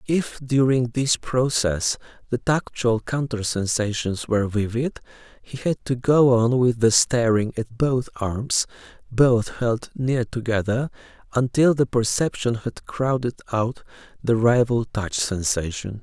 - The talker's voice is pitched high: No, low, 120 Hz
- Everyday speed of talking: No, slow, 130 wpm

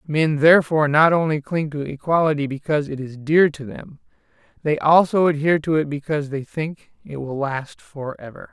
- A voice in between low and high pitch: Yes, medium, 150 Hz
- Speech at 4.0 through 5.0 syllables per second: No, 5.4 syllables/s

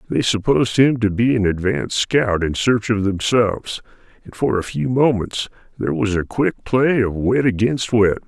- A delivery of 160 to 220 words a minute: Yes, average, 190 wpm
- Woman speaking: No, male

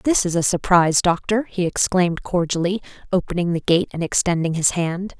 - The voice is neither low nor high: Yes, medium, 180 Hz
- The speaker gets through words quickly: No, average, 175 wpm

